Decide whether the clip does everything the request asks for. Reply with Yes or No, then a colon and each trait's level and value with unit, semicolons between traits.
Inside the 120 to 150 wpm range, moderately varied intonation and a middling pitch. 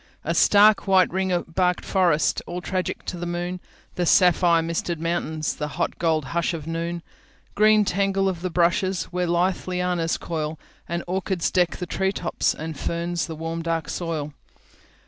No: average, 140 wpm; narrow, 1.9 semitones; medium, 175 Hz